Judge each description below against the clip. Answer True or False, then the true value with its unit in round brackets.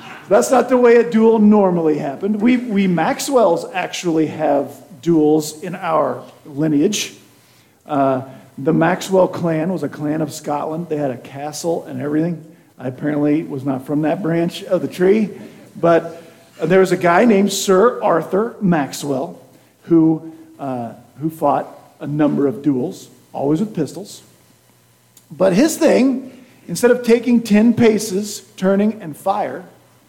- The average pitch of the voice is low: False (165 Hz)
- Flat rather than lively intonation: False (5.3 semitones)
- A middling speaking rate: True (150 wpm)